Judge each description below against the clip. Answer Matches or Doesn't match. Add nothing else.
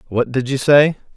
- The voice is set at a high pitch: Doesn't match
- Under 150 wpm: Doesn't match